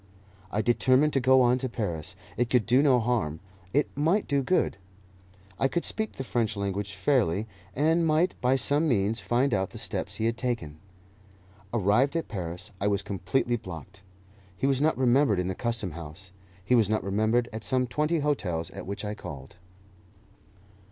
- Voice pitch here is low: Yes, low, 120 Hz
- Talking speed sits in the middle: Yes, average, 180 wpm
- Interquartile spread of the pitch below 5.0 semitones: No, average, 5.3 semitones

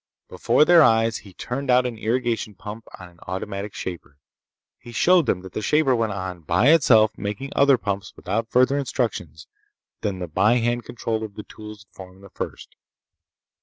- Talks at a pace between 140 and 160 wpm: No, average, 180 wpm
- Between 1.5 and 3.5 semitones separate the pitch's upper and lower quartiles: No, average, 4.1 semitones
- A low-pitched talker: Yes, low, 110 Hz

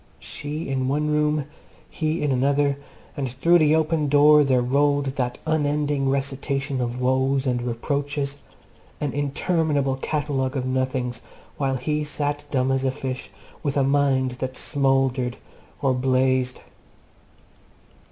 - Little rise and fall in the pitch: Yes, narrow, 2.0 semitones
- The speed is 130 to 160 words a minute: Yes, slow, 135 wpm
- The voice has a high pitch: No, medium, 140 Hz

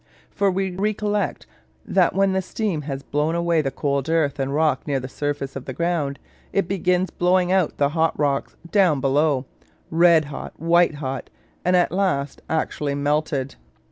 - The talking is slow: No, average, 165 wpm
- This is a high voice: No, medium, 160 Hz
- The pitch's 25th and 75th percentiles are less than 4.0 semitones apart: No, average, 4.3 semitones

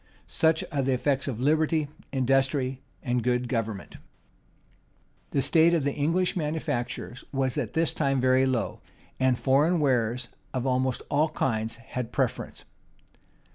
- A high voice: No, low, 135 Hz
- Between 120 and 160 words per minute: Yes, average, 140 wpm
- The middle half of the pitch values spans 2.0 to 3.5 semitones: Yes, average, 3.1 semitones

